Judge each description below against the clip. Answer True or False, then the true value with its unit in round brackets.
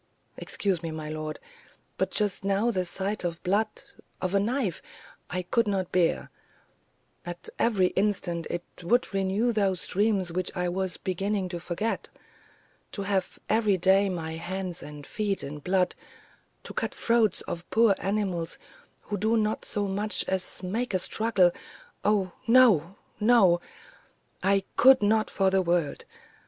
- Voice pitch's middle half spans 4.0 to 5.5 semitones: False (3.1 semitones)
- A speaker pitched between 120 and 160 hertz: False (190 Hz)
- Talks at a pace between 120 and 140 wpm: False (150 wpm)